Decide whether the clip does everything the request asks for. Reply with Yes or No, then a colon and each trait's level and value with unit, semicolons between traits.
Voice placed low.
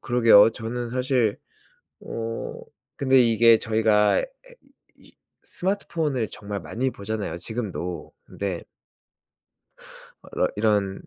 Yes: low, 115 Hz